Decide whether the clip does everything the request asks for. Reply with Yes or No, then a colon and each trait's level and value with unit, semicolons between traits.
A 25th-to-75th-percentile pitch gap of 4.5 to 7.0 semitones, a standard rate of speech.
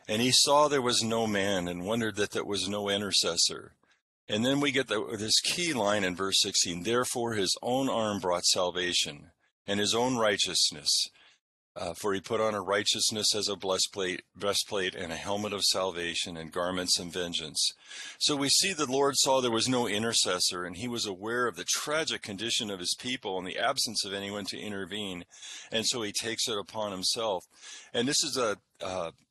No: average, 3.8 semitones; average, 195 wpm